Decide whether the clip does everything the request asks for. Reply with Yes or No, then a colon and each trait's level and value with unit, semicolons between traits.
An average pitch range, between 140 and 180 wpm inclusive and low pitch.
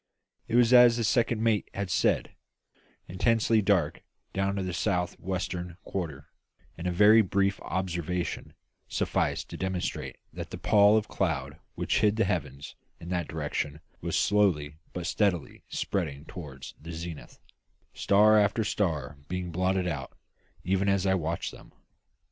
Yes: average, 3.6 semitones; average, 150 wpm; very low, 95 Hz